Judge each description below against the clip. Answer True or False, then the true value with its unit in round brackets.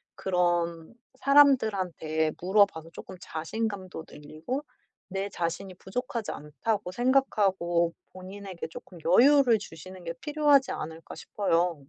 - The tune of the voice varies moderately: True (4.9 semitones)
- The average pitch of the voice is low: False (185 Hz)